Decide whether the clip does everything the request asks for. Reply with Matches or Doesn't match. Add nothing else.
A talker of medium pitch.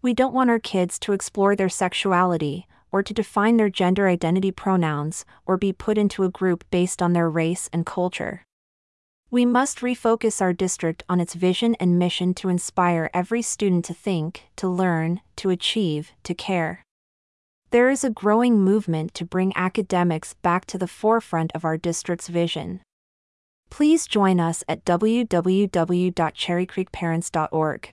Matches